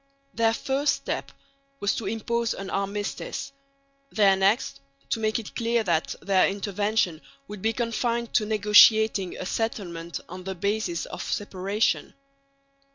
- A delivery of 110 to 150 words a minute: Yes, slow, 135 wpm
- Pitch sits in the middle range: No, high, 210 Hz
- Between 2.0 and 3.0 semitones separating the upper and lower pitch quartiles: Yes, average, 2.7 semitones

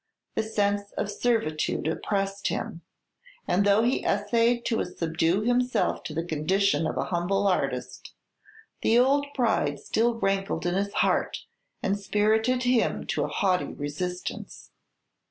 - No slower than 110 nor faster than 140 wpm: Yes, slow, 135 wpm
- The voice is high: Yes, high, 200 Hz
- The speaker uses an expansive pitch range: No, average, 4.4 semitones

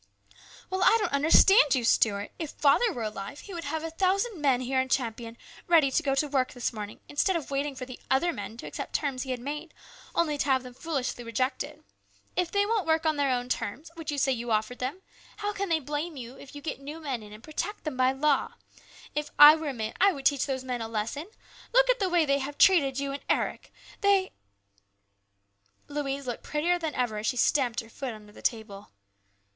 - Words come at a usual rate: No, fast, 230 wpm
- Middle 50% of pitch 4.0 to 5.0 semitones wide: Yes, average, 4.6 semitones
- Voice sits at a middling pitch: No, very high, 275 Hz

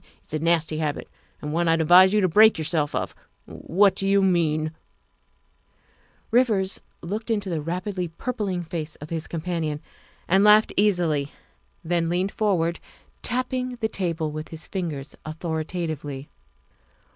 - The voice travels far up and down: No, average, 3.9 semitones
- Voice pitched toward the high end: No, medium, 170 Hz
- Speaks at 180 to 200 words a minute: No, average, 150 wpm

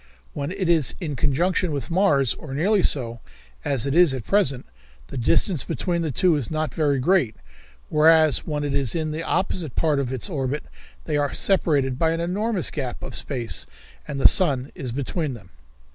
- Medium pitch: Yes, medium, 150 Hz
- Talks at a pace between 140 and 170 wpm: No, average, 190 wpm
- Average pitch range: Yes, average, 4.0 semitones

